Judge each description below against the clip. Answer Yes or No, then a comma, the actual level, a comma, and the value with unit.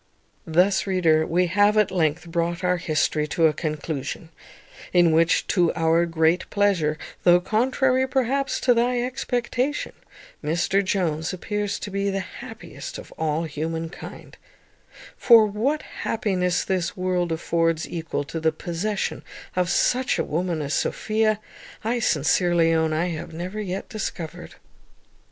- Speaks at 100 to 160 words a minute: Yes, slow, 135 wpm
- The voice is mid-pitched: Yes, medium, 180 Hz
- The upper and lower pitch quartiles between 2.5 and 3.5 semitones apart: No, average, 4.2 semitones